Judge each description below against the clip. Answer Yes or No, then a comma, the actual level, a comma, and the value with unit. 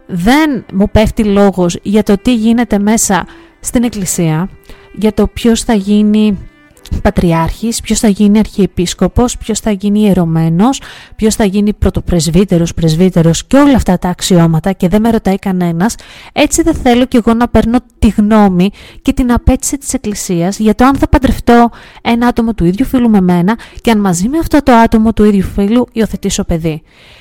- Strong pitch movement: No, average, 4.0 semitones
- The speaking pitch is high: Yes, high, 210 Hz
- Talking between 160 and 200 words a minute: Yes, fast, 170 wpm